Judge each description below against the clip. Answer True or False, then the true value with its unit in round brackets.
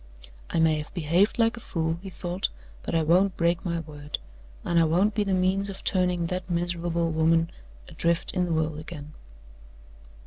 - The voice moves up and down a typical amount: False (2.2 semitones)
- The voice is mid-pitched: True (170 Hz)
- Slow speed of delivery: False (180 wpm)